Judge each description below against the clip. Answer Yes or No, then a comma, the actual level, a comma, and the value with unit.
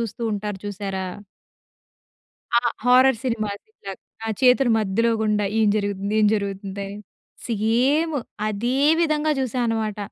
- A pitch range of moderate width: Yes, average, 3.6 semitones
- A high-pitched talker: Yes, high, 215 Hz